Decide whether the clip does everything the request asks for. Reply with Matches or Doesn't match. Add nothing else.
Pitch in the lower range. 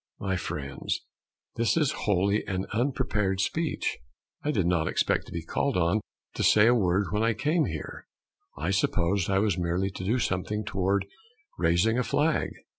Matches